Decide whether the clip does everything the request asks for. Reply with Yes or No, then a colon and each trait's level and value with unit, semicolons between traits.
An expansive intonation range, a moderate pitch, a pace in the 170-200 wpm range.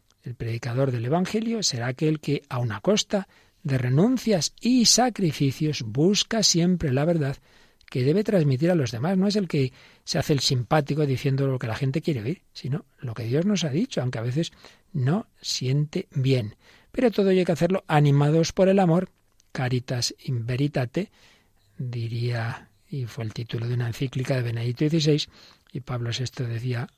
Yes: wide, 5.8 semitones; medium, 145 Hz; average, 175 wpm